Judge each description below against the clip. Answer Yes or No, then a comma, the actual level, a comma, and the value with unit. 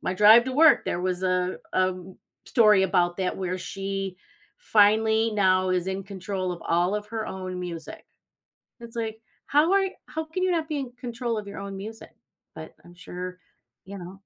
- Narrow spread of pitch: No, average, 3.7 semitones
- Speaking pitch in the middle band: No, high, 195 Hz